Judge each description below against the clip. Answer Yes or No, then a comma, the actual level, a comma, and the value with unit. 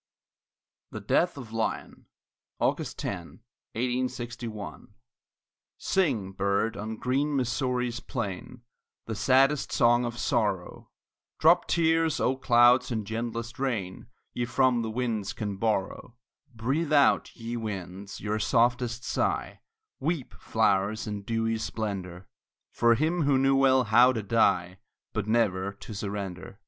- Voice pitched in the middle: No, low, 115 Hz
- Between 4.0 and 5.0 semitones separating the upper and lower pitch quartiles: No, average, 3.5 semitones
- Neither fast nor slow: No, slow, 125 wpm